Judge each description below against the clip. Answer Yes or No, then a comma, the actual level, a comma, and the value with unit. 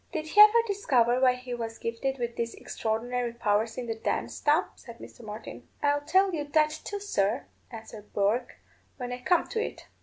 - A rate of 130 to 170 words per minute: No, average, 190 wpm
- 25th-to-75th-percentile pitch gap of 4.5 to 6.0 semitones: Yes, average, 5.0 semitones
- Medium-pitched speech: No, high, 245 Hz